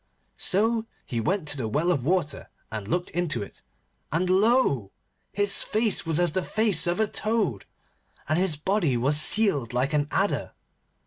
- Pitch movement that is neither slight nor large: No, wide, 6.1 semitones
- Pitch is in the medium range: Yes, medium, 175 Hz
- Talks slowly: No, average, 170 wpm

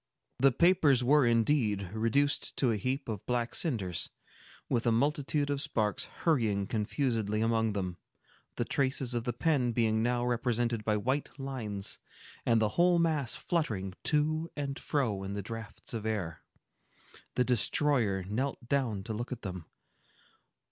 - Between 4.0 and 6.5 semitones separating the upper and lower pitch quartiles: Yes, average, 4.5 semitones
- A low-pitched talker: Yes, low, 120 Hz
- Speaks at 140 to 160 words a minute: Yes, average, 150 wpm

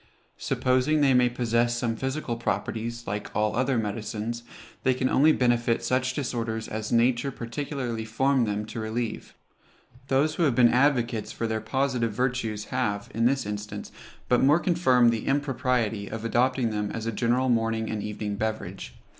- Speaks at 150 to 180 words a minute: Yes, average, 165 wpm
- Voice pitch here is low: Yes, low, 120 Hz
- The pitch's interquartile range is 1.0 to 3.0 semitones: Yes, narrow, 2.6 semitones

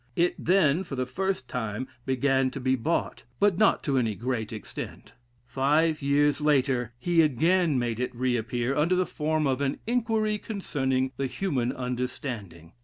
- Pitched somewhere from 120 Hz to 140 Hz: Yes, low, 135 Hz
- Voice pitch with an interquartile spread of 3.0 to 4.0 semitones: No, average, 4.7 semitones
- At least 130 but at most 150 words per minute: No, average, 165 wpm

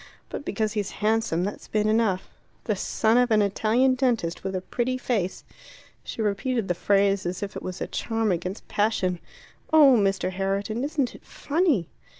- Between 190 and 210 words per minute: No, average, 170 wpm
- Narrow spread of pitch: No, average, 3.7 semitones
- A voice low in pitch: No, high, 210 Hz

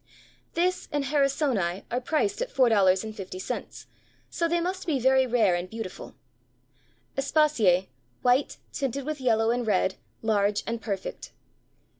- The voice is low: No, high, 245 Hz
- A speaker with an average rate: No, slow, 125 wpm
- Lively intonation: Yes, wide, 6.0 semitones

